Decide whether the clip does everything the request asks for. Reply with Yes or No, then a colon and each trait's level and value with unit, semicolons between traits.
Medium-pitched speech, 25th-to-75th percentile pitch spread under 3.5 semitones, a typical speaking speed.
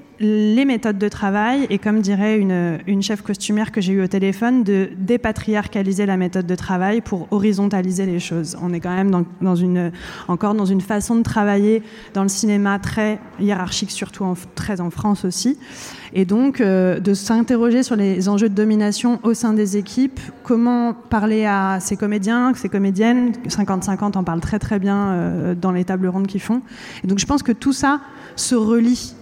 No: high, 205 Hz; average, 2.9 semitones; average, 190 wpm